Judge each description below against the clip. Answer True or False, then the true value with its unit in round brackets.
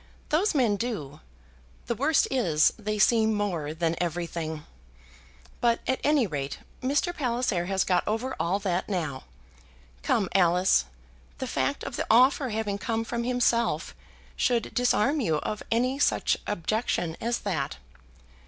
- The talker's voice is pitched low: False (215 Hz)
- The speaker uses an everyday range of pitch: False (5.9 semitones)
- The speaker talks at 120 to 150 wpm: True (140 wpm)